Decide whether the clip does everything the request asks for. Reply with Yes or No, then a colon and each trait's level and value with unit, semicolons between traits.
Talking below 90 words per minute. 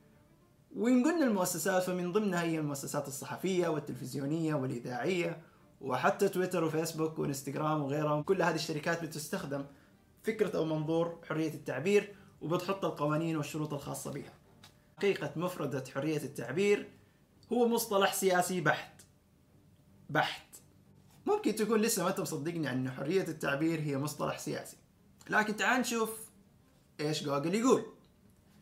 No: average, 115 wpm